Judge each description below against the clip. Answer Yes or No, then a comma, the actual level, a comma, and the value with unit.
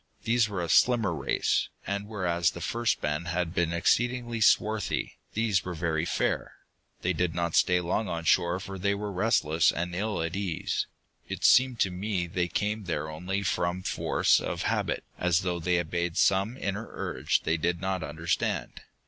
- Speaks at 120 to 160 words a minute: No, average, 175 wpm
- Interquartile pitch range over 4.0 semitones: No, average, 3.3 semitones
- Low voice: Yes, very low, 90 Hz